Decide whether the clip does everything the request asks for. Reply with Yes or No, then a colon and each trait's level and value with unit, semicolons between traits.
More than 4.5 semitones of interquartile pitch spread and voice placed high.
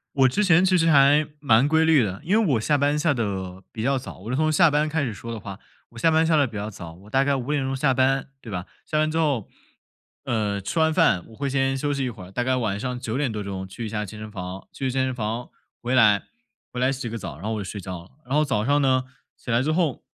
No: wide, 5.4 semitones; low, 130 Hz